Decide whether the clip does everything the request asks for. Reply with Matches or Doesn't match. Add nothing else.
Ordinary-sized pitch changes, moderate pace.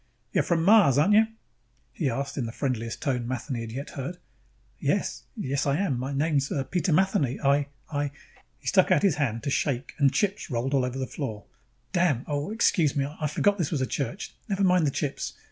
Doesn't match